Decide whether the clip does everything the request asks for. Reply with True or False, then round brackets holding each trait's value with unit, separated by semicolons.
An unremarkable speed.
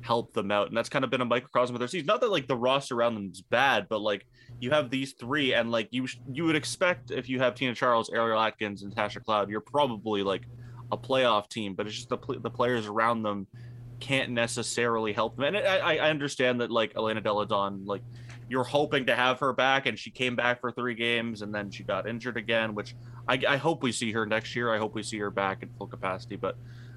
False (245 wpm)